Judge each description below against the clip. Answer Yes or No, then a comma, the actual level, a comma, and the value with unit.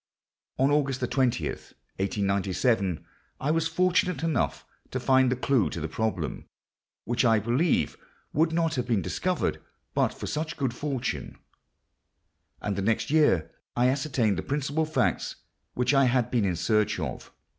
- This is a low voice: Yes, low, 125 Hz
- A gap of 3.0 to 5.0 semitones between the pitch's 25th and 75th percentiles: No, wide, 5.4 semitones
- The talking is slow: No, average, 145 wpm